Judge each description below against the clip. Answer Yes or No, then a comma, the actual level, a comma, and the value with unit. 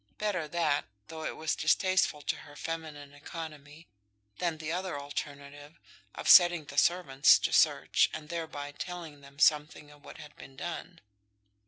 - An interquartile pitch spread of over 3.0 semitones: No, average, 2.7 semitones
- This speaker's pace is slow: No, average, 155 wpm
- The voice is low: No, medium, 155 Hz